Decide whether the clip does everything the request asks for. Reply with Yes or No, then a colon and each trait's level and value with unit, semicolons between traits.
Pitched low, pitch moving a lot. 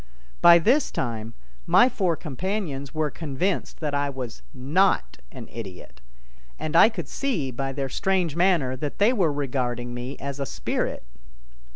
No: medium, 145 Hz; wide, 5.8 semitones